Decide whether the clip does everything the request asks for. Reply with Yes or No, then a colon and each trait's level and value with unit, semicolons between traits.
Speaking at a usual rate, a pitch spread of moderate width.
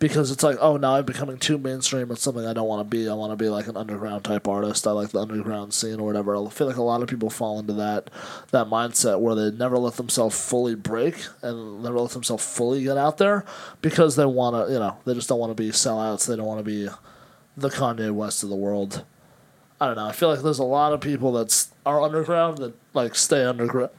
No: fast, 255 wpm; average, 4.1 semitones